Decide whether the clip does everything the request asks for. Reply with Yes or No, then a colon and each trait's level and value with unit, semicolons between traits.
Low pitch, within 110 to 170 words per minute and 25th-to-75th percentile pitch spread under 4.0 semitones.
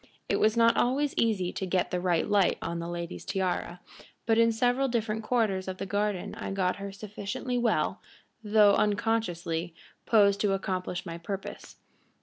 No: high, 200 Hz; average, 165 wpm; average, 3.6 semitones